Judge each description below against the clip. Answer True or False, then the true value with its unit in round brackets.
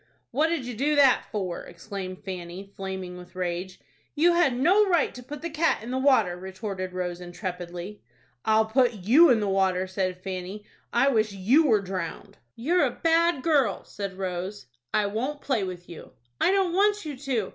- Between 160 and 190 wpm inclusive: True (185 wpm)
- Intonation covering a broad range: True (7.0 semitones)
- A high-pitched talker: True (210 Hz)